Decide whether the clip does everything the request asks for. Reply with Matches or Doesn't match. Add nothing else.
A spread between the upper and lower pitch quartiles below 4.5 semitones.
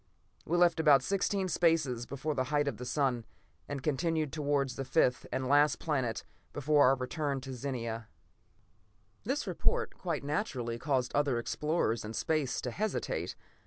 Matches